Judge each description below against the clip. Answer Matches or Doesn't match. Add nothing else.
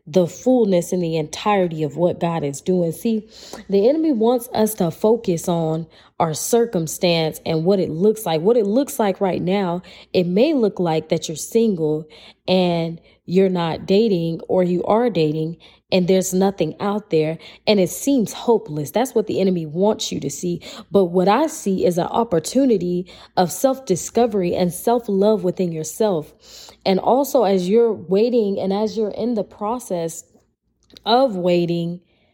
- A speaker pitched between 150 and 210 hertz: Matches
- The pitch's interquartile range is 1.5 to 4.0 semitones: Doesn't match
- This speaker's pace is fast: Doesn't match